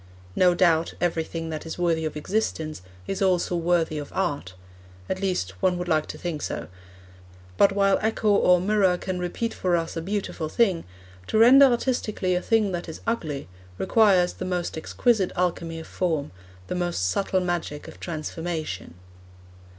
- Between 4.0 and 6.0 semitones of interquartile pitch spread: No, average, 3.1 semitones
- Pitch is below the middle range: No, medium, 175 Hz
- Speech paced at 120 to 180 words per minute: Yes, average, 165 wpm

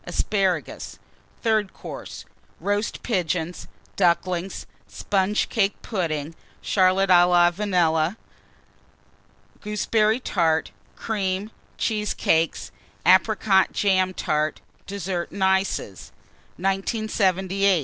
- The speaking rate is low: Yes, slow, 80 wpm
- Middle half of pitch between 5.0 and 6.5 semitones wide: No, average, 2.7 semitones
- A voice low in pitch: No, high, 190 Hz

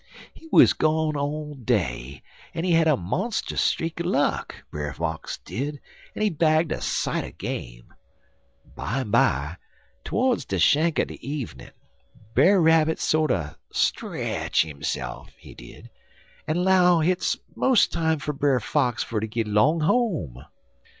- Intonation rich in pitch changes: Yes, wide, 8.8 semitones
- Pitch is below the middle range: No, medium, 150 Hz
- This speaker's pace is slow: No, average, 145 wpm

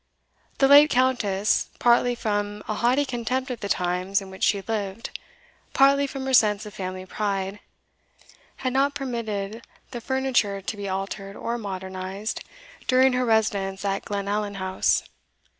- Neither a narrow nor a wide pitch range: Yes, average, 4.2 semitones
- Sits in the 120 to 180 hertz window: No, high, 210 Hz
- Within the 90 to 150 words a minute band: Yes, average, 145 wpm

